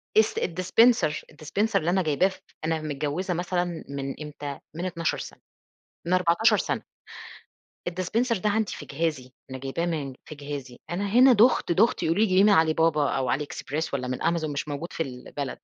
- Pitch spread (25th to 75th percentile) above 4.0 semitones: Yes, average, 4.4 semitones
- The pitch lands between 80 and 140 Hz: No, medium, 165 Hz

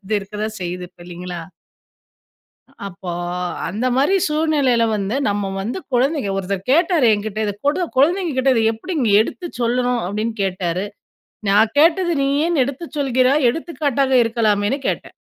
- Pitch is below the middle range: No, high, 240 Hz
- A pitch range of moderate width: No, wide, 6.0 semitones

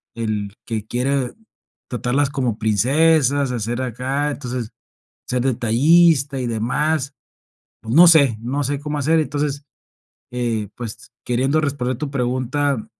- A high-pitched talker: No, low, 130 Hz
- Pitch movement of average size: Yes, average, 3.3 semitones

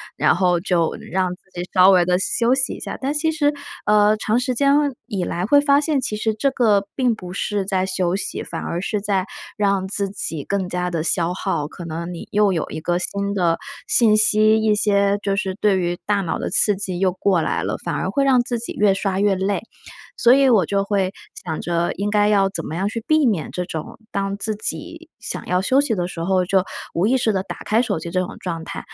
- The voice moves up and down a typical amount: Yes, average, 3.1 semitones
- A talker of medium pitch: No, high, 200 Hz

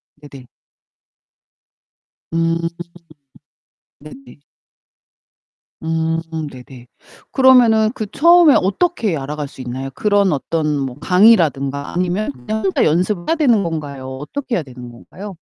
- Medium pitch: Yes, medium, 165 Hz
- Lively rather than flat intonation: Yes, wide, 7.4 semitones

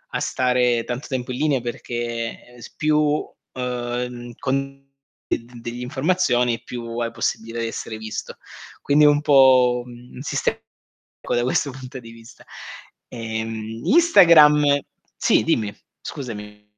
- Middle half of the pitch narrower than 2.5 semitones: No, average, 2.8 semitones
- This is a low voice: Yes, low, 125 Hz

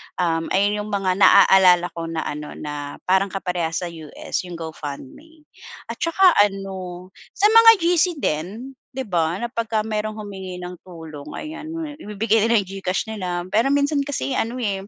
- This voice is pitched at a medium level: No, high, 195 Hz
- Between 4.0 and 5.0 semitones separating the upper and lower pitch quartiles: Yes, average, 4.7 semitones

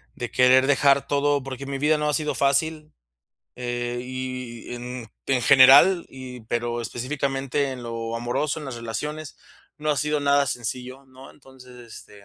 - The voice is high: No, low, 130 Hz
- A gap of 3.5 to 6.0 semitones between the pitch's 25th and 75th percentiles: No, average, 2.7 semitones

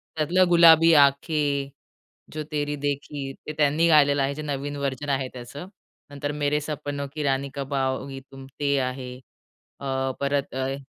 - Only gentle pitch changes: Yes, narrow, 1.6 semitones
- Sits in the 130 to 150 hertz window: Yes, medium, 140 Hz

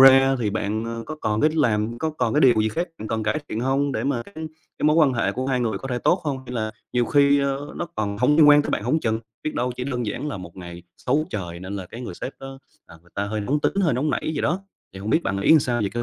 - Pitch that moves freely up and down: No, average, 4.8 semitones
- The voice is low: Yes, low, 125 Hz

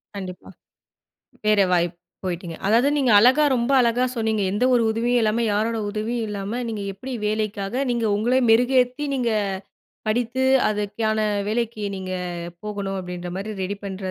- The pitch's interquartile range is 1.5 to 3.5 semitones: Yes, average, 3.1 semitones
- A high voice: Yes, high, 220 Hz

